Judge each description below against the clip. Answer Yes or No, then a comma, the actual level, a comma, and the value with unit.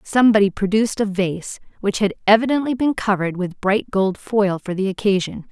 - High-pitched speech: Yes, high, 205 Hz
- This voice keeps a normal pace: Yes, average, 175 wpm